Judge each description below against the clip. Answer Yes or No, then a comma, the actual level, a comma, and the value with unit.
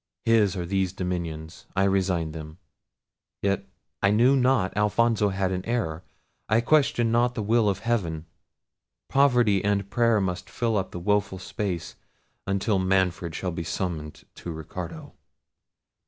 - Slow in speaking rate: Yes, slow, 130 wpm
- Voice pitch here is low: Yes, very low, 95 Hz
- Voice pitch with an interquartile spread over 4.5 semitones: No, average, 4.0 semitones